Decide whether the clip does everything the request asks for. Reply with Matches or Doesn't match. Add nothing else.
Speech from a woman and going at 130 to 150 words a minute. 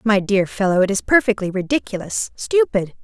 Matches